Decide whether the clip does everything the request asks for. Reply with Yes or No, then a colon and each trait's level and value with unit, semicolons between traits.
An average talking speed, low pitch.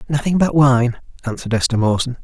Yes: average, 160 wpm; low, 130 Hz